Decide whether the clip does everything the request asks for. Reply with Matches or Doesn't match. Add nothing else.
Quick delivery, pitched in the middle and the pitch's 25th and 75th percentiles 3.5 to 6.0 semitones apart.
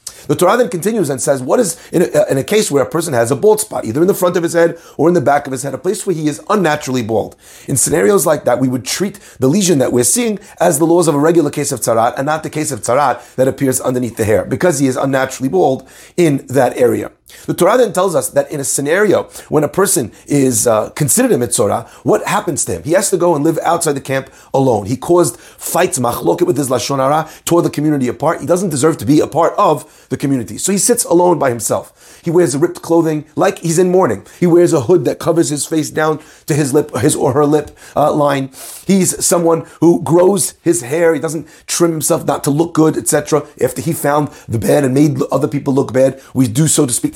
Matches